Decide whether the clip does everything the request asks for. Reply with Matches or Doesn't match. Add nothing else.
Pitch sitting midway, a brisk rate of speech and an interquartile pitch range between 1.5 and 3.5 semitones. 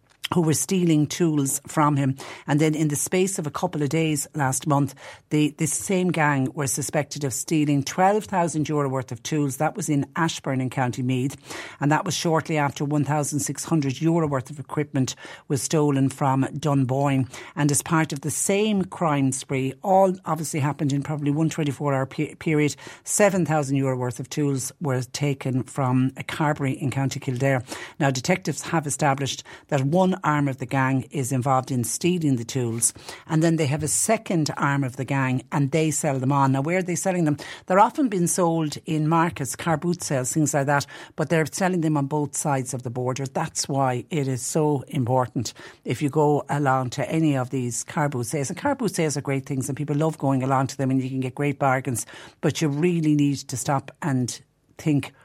Matches